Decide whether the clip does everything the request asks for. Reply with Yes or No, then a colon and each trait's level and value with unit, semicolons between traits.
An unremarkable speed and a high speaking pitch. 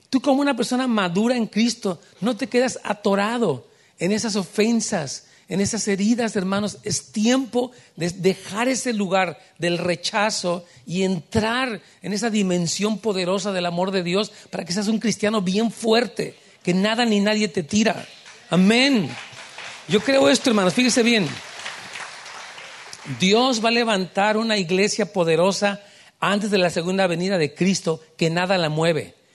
Yes: average, 150 wpm; high, 205 Hz